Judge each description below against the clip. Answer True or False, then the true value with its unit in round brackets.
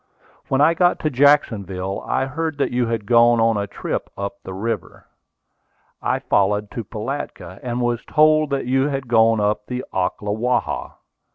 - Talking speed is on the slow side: False (165 wpm)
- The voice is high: False (120 Hz)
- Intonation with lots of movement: False (4.8 semitones)